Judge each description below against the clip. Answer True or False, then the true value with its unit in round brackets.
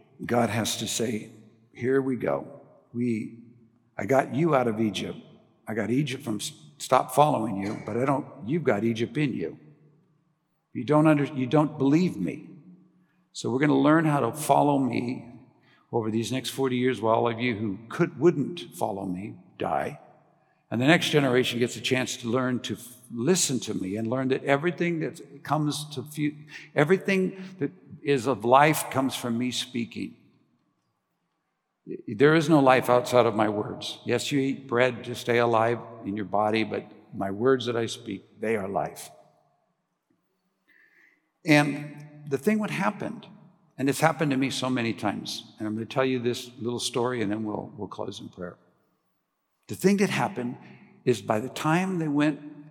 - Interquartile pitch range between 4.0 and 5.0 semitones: True (4.3 semitones)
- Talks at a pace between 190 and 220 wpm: False (180 wpm)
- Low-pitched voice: True (130 Hz)